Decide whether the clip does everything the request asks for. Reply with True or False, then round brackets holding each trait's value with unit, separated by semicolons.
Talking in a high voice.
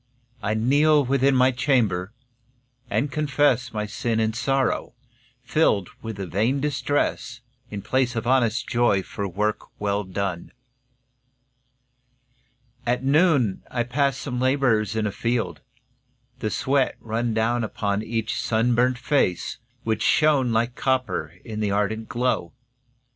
False (120 Hz)